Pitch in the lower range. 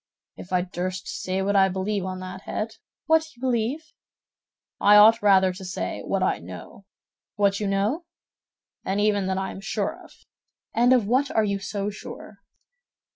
No: high, 200 Hz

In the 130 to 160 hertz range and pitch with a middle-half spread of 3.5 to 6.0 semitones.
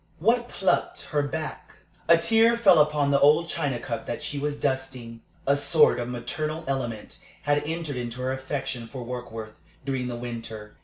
Yes: medium, 140 Hz; average, 3.9 semitones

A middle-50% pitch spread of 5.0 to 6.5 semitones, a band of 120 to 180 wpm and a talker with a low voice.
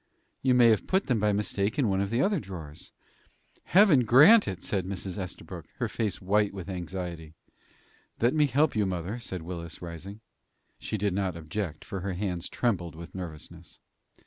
No: average, 4.6 semitones; average, 175 wpm; low, 100 Hz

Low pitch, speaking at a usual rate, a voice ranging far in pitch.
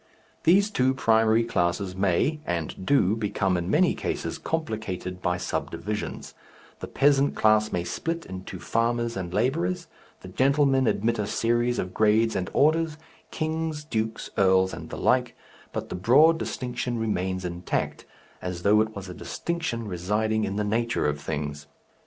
Yes: low, 110 Hz; average, 150 wpm; wide, 6.3 semitones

